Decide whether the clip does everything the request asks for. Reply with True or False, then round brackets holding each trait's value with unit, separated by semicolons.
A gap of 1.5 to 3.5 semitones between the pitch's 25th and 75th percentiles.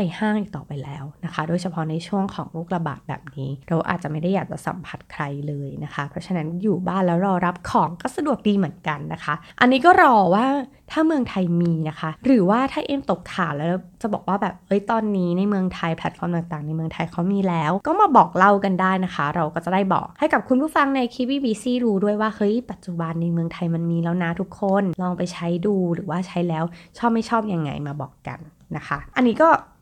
False (4.2 semitones)